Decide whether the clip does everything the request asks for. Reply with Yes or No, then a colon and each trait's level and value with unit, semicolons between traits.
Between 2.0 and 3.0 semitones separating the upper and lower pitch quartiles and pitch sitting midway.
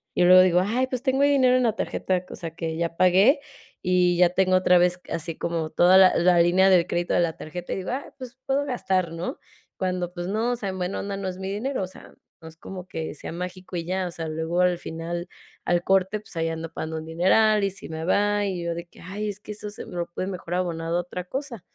Yes: average, 2.7 semitones; medium, 180 Hz